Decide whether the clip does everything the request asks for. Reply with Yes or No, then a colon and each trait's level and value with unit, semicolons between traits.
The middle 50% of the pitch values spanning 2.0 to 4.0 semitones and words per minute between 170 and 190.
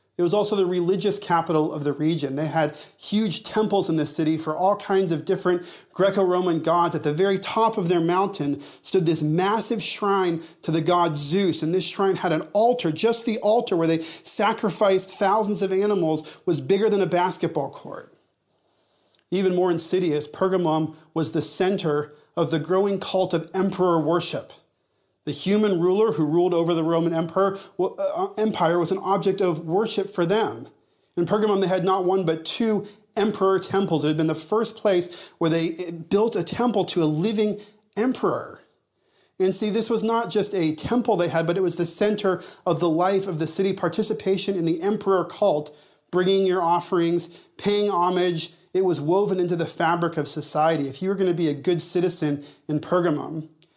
Yes: average, 3.2 semitones; average, 185 wpm